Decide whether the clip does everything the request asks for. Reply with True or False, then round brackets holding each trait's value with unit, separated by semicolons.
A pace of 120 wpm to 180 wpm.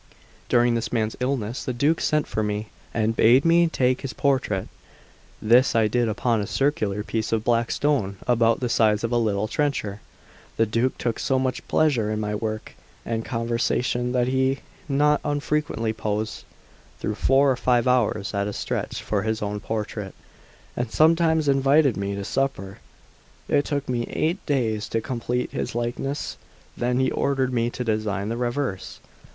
True (170 wpm)